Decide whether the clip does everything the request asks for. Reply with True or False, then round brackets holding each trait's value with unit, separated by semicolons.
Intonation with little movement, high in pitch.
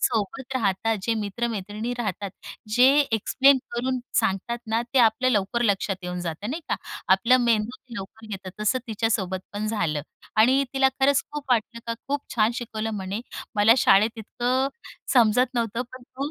False (3.4 semitones; 225 Hz)